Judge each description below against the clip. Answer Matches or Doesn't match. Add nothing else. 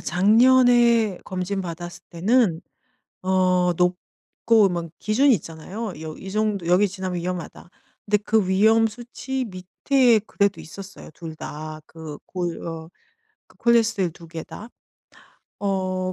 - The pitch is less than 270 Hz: Matches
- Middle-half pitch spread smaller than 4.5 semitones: Matches